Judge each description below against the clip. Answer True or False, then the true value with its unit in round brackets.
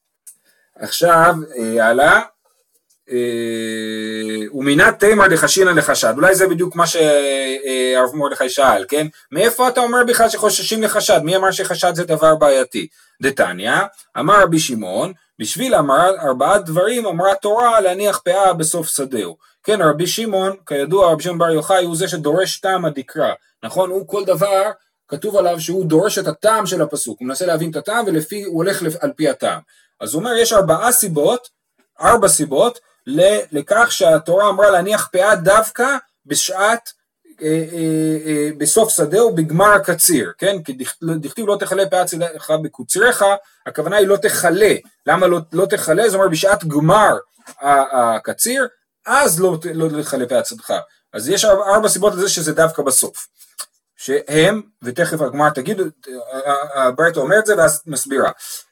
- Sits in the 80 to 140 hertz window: False (180 Hz)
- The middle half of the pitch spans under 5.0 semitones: False (5.3 semitones)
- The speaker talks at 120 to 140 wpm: False (150 wpm)